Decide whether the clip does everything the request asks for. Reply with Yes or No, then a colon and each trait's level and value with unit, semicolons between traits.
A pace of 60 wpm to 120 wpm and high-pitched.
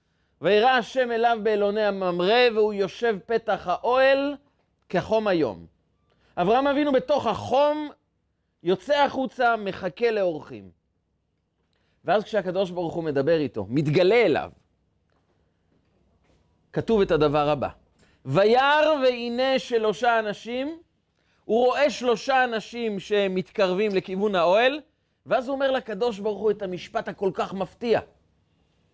Yes: average, 110 wpm; high, 205 Hz